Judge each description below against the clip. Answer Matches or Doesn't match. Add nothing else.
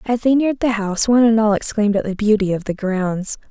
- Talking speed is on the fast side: Matches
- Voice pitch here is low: Doesn't match